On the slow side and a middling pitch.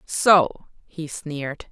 Yes: slow, 105 wpm; medium, 160 Hz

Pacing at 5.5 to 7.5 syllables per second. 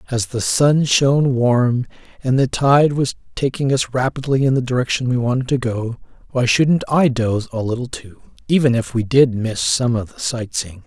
No: 4.9 syllables/s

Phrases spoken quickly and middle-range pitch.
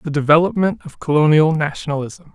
No: slow, 130 wpm; medium, 155 Hz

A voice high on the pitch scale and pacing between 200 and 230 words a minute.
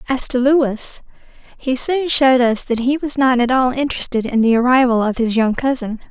Yes: very high, 250 Hz; fast, 205 wpm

